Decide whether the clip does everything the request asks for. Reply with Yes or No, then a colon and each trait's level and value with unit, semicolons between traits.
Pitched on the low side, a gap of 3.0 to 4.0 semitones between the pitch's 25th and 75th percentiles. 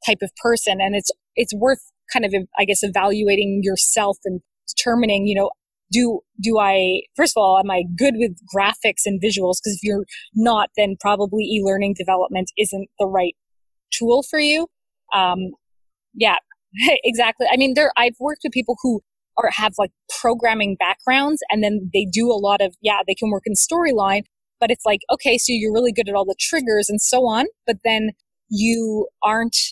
No: high, 210 Hz; average, 3.3 semitones